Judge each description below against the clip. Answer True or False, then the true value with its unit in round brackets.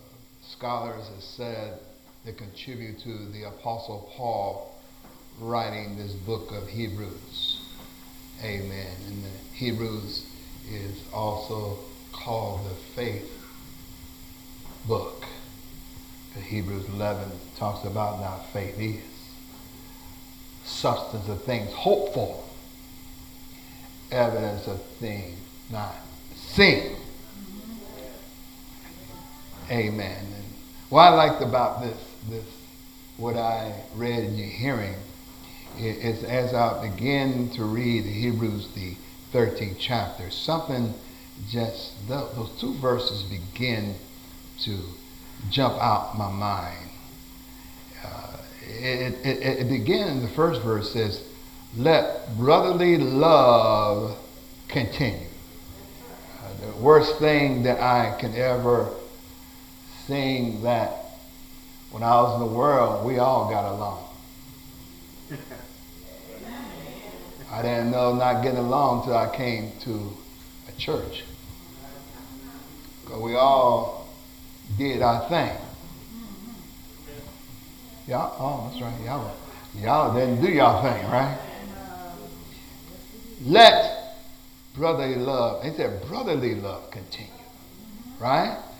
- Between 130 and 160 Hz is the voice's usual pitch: False (115 Hz)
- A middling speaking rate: False (100 wpm)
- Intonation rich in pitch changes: False (4.2 semitones)